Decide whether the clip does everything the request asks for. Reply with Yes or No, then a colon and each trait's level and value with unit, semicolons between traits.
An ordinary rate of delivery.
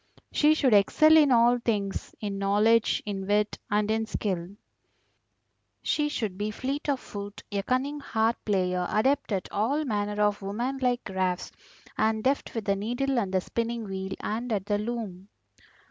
Yes: average, 165 wpm